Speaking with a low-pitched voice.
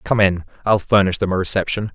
Yes: very low, 95 Hz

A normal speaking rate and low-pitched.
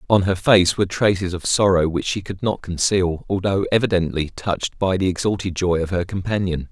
Yes: average, 195 wpm; very low, 95 Hz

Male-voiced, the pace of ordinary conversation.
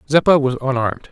Yes: male; average, 160 wpm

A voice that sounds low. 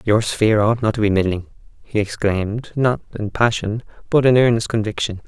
Yes: low, 110 Hz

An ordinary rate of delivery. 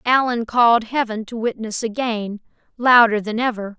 Yes: average, 145 wpm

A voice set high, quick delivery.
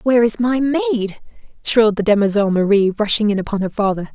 No: high, 210 Hz; average, 190 wpm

